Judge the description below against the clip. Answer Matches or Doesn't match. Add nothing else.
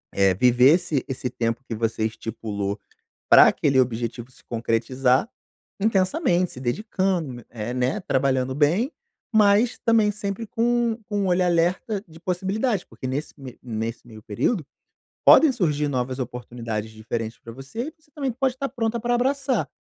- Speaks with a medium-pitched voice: Matches